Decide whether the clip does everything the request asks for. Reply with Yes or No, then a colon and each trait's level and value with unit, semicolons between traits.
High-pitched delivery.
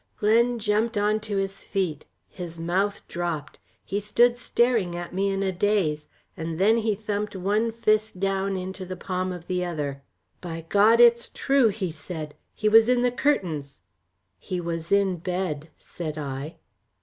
Yes: high, 195 Hz